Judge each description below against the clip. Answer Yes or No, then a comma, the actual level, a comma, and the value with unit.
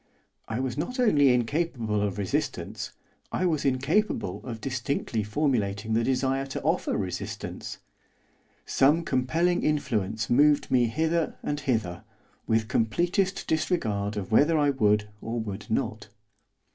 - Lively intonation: Yes, wide, 5.7 semitones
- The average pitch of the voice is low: Yes, low, 130 Hz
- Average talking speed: No, slow, 130 wpm